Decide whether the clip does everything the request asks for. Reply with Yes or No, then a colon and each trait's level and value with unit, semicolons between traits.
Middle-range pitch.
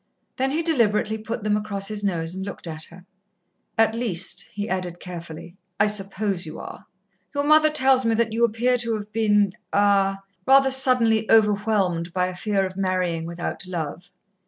No: high, 205 Hz